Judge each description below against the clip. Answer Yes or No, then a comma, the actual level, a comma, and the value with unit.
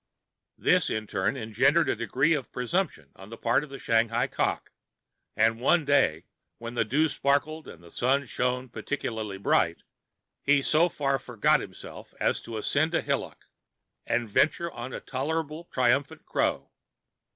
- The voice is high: No, low, 130 Hz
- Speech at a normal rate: Yes, average, 160 wpm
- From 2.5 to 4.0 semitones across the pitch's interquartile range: No, average, 4.5 semitones